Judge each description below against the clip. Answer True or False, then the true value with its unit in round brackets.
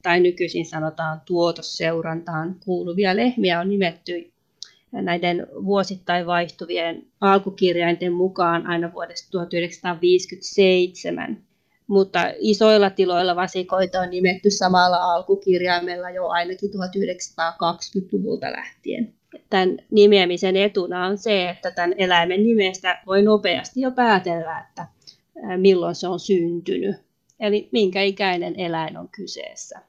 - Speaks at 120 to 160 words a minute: False (105 wpm)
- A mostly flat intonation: True (2.1 semitones)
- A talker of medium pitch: True (180 Hz)